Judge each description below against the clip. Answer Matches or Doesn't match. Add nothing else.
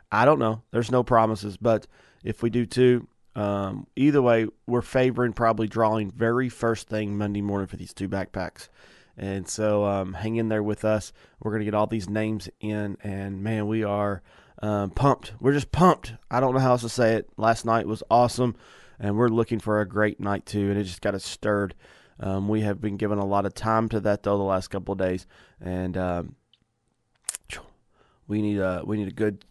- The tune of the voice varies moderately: Doesn't match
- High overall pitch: Doesn't match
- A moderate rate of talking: Doesn't match